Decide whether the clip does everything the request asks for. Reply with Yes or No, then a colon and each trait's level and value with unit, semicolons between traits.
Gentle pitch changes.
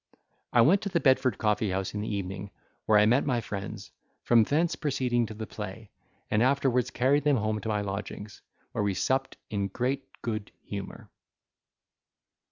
No: average, 4.3 semitones